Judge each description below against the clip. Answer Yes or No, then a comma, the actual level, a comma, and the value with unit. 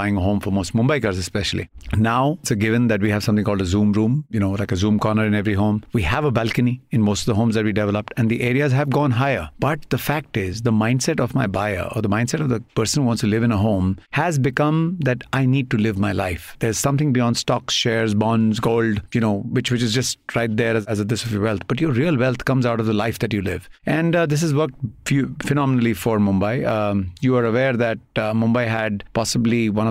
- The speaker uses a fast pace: Yes, fast, 265 wpm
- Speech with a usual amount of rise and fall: Yes, average, 3.5 semitones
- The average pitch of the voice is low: Yes, low, 115 Hz